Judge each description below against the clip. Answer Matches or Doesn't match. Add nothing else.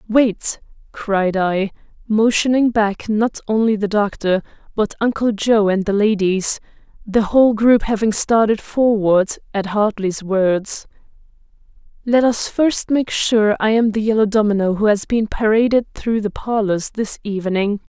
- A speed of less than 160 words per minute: Matches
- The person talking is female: Matches